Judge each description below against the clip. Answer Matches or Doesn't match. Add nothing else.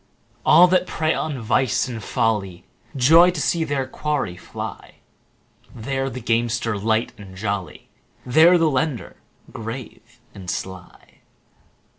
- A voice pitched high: Doesn't match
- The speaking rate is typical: Doesn't match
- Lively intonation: Matches